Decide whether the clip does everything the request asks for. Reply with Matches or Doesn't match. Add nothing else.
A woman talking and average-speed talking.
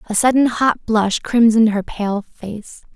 Matches